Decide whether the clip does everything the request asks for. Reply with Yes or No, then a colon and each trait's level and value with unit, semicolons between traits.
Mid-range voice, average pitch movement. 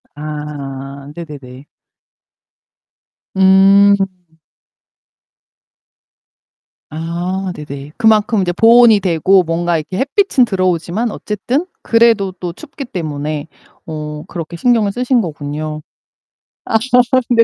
No: medium, 175 Hz; wide, 6.0 semitones